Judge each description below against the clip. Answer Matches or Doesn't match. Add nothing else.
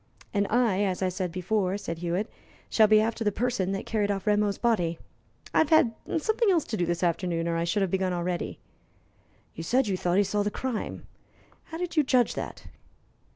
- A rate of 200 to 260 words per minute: Matches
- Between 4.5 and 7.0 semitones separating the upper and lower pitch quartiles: Doesn't match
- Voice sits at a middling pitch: Doesn't match